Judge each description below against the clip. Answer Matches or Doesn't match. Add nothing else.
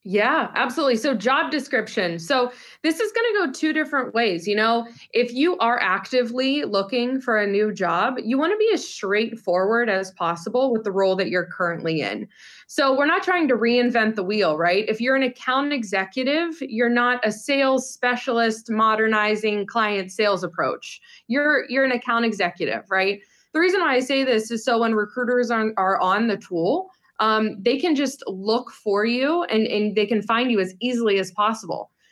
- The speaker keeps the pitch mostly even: Doesn't match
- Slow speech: Doesn't match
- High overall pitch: Matches